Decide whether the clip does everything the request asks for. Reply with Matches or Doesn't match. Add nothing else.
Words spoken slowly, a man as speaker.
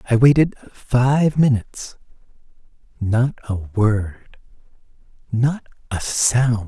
Matches